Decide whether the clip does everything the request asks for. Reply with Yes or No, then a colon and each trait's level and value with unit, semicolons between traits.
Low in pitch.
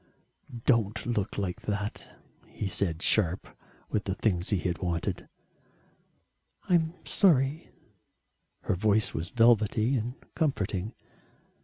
Yes: low, 105 Hz